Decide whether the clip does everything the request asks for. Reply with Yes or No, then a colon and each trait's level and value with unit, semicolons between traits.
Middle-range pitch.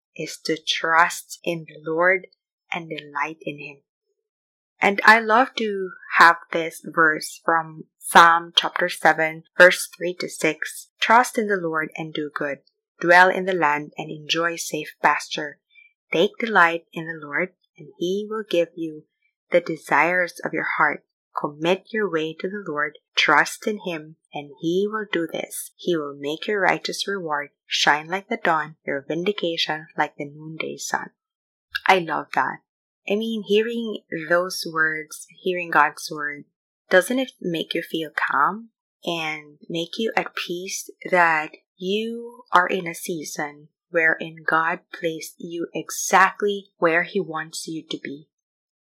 Yes: medium, 170 Hz